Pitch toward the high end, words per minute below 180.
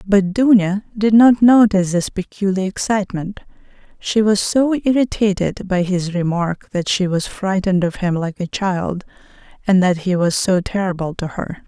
Yes: high, 195 Hz; average, 165 wpm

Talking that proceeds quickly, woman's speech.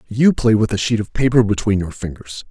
No: fast, 240 wpm; male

